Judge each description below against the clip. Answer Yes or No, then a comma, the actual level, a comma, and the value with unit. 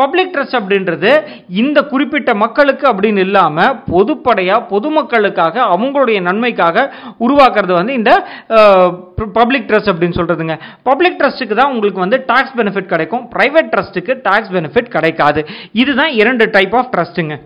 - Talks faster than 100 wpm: Yes, average, 125 wpm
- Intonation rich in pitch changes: Yes, wide, 6.1 semitones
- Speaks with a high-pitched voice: Yes, high, 225 Hz